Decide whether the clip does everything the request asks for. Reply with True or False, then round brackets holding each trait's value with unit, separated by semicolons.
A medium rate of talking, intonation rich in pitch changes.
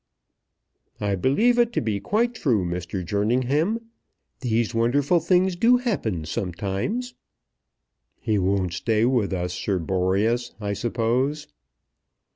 False (115 wpm; 7.8 semitones)